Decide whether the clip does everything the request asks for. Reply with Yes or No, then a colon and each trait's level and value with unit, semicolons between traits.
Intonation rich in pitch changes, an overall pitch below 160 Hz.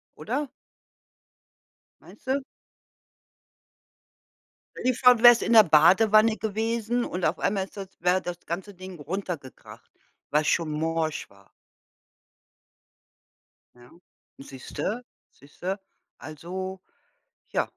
No: wide, 5.8 semitones; medium, 185 Hz